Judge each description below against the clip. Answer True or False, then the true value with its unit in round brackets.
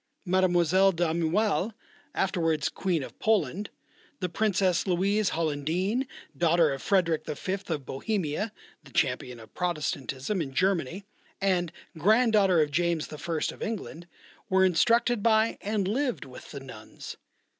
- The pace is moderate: False (130 wpm)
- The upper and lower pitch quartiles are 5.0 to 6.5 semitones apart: False (4.2 semitones)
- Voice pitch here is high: False (180 Hz)